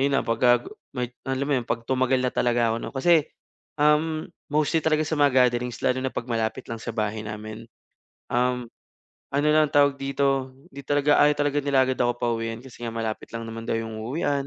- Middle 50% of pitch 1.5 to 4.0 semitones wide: Yes, average, 3.6 semitones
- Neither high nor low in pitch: No, low, 130 Hz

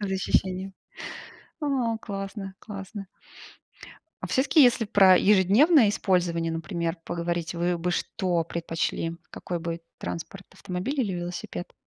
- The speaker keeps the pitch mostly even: No, average, 3.2 semitones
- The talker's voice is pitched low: No, high, 190 Hz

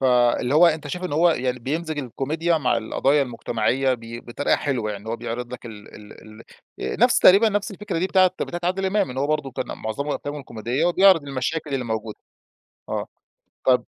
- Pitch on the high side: No, low, 135 Hz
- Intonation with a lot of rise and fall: Yes, wide, 5.8 semitones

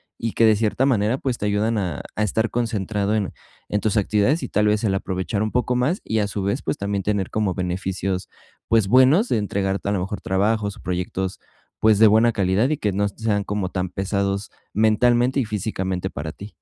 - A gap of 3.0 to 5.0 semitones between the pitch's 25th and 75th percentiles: No, narrow, 2.5 semitones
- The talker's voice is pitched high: No, low, 105 Hz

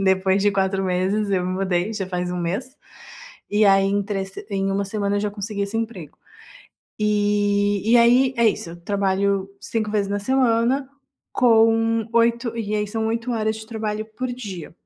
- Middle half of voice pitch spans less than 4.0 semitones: Yes, average, 2.7 semitones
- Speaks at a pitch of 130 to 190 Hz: No, high, 205 Hz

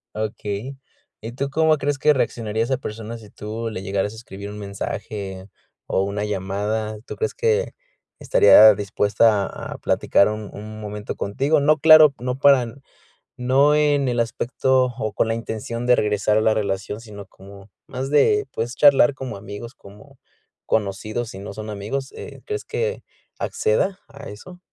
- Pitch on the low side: Yes, low, 110 Hz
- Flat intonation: No, average, 4.9 semitones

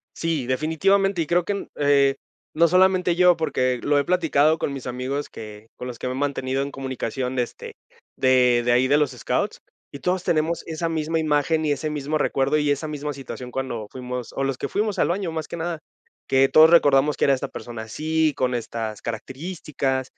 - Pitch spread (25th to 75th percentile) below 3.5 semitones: No, average, 3.8 semitones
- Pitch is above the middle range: No, medium, 145 Hz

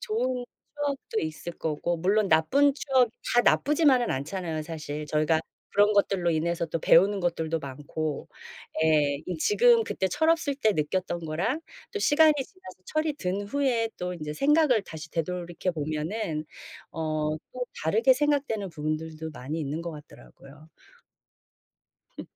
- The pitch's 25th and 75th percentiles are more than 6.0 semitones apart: Yes, wide, 8.5 semitones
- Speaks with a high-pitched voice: No, medium, 180 Hz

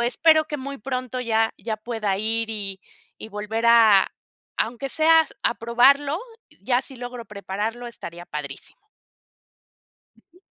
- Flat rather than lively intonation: No, average, 3.2 semitones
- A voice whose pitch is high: Yes, high, 235 Hz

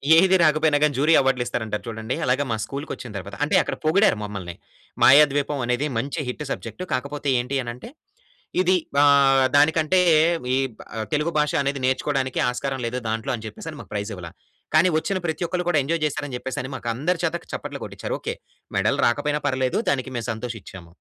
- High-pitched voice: No, medium, 140 Hz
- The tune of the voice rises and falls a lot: No, average, 3.8 semitones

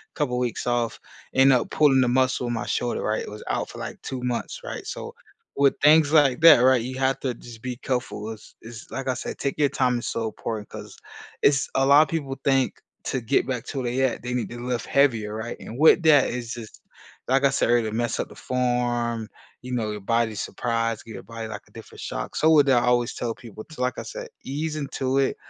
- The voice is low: Yes, low, 125 Hz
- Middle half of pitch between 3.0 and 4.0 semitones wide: No, narrow, 2.6 semitones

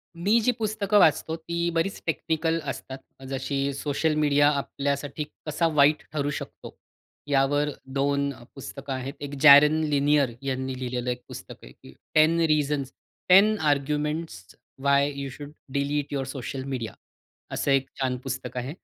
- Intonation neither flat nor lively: No, narrow, 2.2 semitones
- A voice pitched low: No, medium, 145 Hz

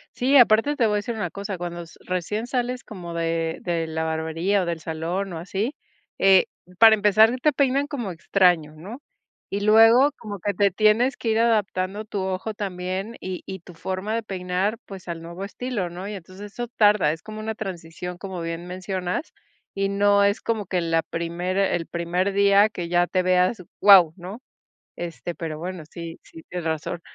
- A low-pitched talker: No, high, 190 Hz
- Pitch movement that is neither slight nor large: Yes, average, 3.6 semitones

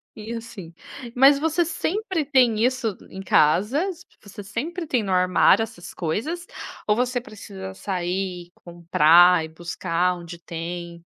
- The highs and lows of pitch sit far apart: Yes, wide, 6.5 semitones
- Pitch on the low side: No, high, 200 Hz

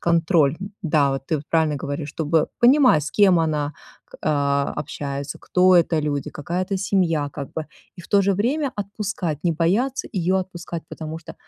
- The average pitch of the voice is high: No, medium, 165 Hz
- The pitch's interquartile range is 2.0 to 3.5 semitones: No, average, 4.1 semitones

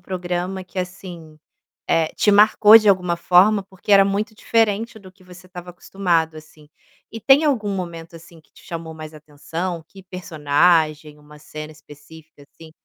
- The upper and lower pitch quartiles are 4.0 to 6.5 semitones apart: No, average, 3.6 semitones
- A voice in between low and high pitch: Yes, medium, 180 Hz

